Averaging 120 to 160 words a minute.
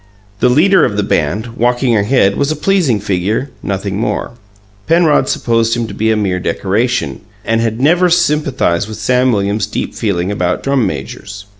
No: average, 170 wpm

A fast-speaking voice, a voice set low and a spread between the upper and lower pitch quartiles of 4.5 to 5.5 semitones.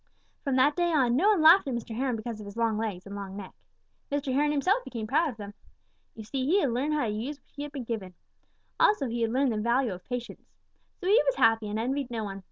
No: fast, 260 wpm; high, 245 Hz; average, 4.9 semitones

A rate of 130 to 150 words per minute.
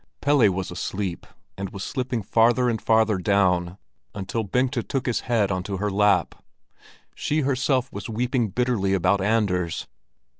Yes: average, 145 wpm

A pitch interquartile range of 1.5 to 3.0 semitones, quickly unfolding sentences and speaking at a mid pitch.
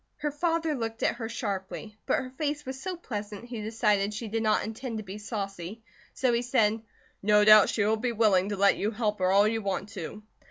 No: average, 2.7 semitones; fast, 225 wpm; high, 215 Hz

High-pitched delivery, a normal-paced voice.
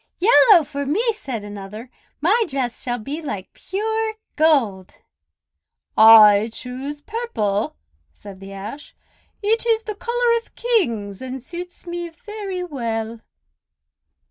No: very high, 285 Hz; slow, 120 wpm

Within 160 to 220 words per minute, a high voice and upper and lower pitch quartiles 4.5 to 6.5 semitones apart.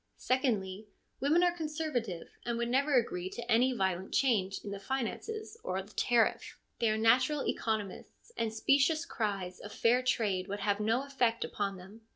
Yes: average, 175 wpm; high, 230 Hz; average, 4.8 semitones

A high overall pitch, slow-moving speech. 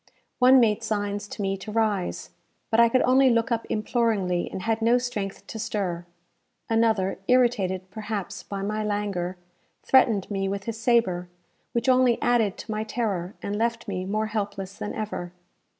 No: high, 215 Hz; average, 165 wpm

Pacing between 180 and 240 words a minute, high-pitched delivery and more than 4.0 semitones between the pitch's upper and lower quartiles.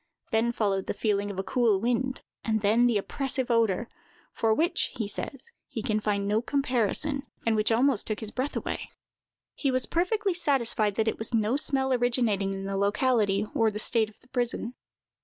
No: average, 190 wpm; high, 230 Hz; average, 3.5 semitones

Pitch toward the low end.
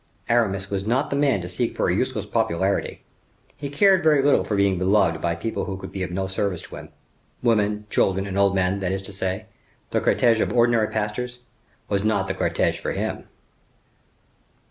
Yes: low, 100 Hz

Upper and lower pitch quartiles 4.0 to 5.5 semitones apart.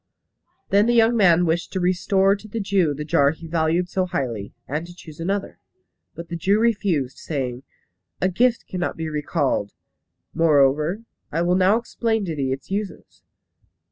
Yes: average, 4.7 semitones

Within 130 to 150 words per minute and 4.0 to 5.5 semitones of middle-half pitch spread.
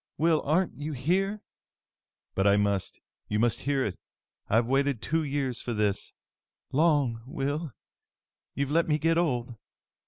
Yes: average, 145 wpm; average, 5.0 semitones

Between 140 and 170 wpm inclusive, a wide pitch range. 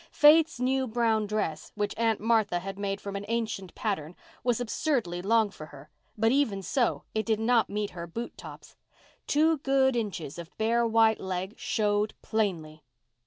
No: average, 165 wpm; average, 3.3 semitones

